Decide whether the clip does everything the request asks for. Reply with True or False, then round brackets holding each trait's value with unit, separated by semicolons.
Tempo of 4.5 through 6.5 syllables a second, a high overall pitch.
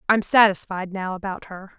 True (5.0 syllables/s; 195 Hz)